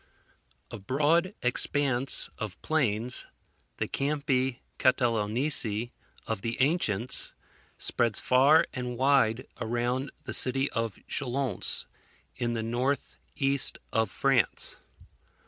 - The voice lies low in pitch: Yes, low, 125 Hz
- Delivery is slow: Yes, slow, 100 wpm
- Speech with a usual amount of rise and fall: Yes, average, 3.1 semitones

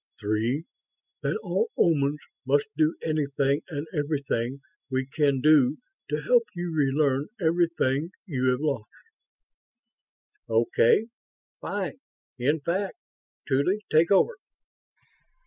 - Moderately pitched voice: Yes, medium, 145 Hz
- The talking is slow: Yes, slow, 105 wpm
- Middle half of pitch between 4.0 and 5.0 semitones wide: No, average, 3.5 semitones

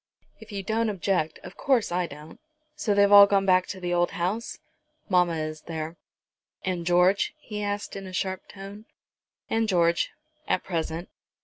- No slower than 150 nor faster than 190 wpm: Yes, average, 170 wpm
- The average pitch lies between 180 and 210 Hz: Yes, medium, 185 Hz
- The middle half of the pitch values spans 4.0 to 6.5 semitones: No, average, 2.8 semitones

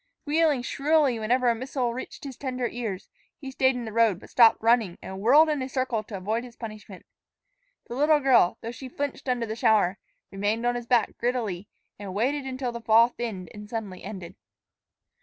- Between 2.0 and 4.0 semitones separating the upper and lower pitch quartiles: Yes, average, 3.3 semitones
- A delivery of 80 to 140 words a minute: No, average, 195 wpm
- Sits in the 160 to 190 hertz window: No, high, 235 Hz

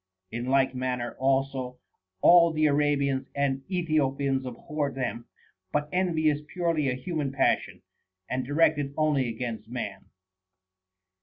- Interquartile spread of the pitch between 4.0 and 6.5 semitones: No, average, 3.0 semitones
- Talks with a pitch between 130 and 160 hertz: Yes, medium, 140 Hz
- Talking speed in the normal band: No, slow, 125 wpm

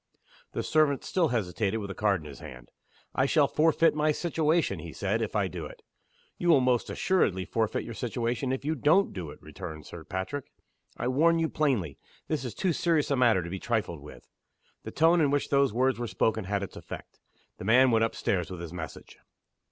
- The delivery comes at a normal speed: No, fast, 210 wpm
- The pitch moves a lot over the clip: Yes, wide, 7.7 semitones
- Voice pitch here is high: No, low, 125 Hz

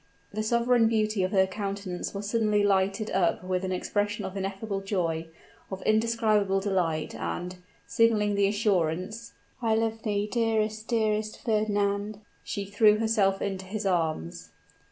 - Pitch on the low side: No, high, 205 Hz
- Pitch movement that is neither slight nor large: No, narrow, 2.2 semitones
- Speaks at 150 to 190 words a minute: No, average, 140 wpm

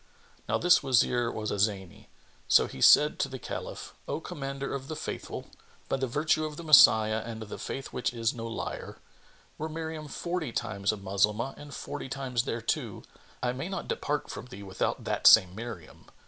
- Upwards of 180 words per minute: Yes, average, 190 wpm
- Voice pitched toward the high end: No, low, 125 Hz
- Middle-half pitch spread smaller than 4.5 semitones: No, average, 5.0 semitones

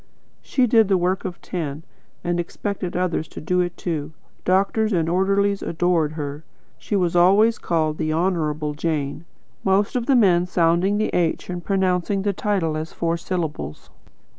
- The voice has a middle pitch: Yes, medium, 175 Hz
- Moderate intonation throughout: Yes, average, 3.2 semitones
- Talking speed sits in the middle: Yes, average, 165 wpm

